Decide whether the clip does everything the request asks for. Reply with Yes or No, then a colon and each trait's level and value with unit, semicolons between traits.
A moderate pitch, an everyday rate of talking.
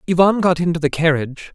Yes: medium, 165 Hz; average, 195 wpm